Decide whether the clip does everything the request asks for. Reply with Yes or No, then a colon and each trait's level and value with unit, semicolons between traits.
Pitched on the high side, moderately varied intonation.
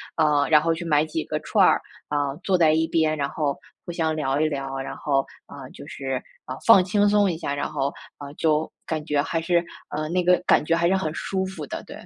No: medium, 155 Hz; average, 3.0 semitones